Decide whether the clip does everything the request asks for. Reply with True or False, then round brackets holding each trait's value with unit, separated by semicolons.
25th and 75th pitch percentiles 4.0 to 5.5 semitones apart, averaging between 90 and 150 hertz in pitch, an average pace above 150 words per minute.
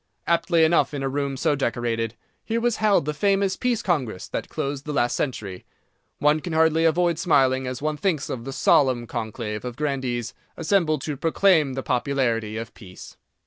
True (5.1 semitones; 140 Hz; 180 wpm)